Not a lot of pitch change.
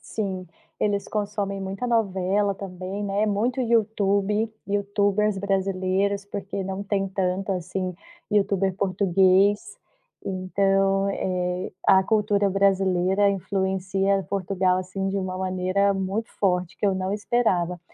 Yes: narrow, 1.3 semitones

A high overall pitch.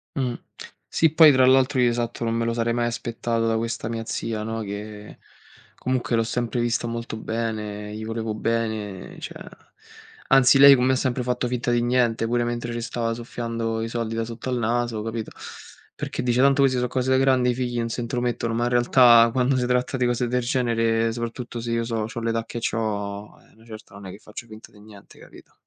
No: low, 115 Hz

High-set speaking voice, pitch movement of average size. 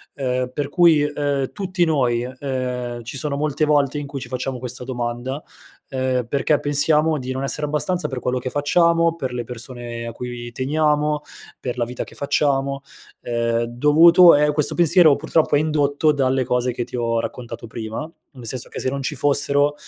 No: low, 135 Hz; average, 3.1 semitones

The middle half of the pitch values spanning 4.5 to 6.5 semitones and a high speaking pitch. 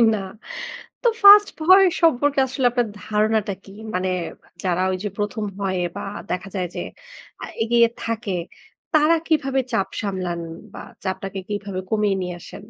Yes: wide, 5.4 semitones; high, 210 Hz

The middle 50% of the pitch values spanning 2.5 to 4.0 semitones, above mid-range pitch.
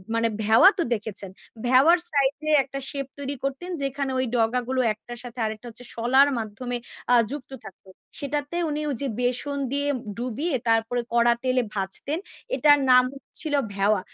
Yes: average, 3.6 semitones; very high, 255 Hz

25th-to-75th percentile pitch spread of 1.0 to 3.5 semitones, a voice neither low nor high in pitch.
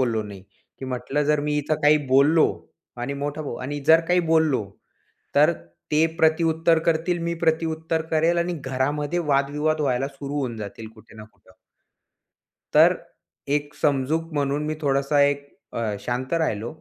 Yes: average, 3.2 semitones; medium, 145 Hz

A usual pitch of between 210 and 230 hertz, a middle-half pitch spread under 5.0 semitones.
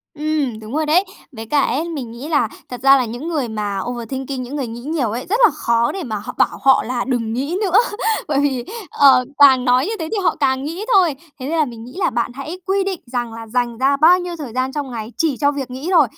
No: very high, 270 Hz; average, 4.3 semitones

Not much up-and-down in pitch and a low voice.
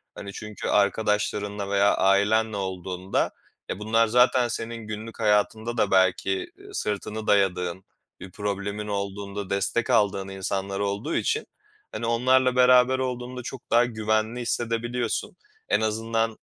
No: average, 3.0 semitones; low, 110 Hz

